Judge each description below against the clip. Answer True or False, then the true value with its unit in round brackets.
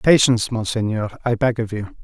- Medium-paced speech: True (175 wpm)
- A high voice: False (115 Hz)